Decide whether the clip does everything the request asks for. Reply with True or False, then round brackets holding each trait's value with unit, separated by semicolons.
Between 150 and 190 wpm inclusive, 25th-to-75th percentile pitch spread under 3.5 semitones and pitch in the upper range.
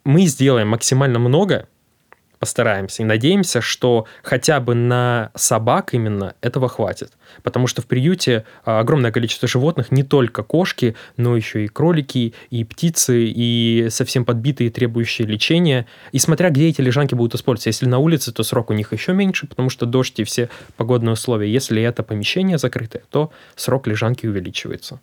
False (160 wpm; 2.8 semitones; 125 Hz)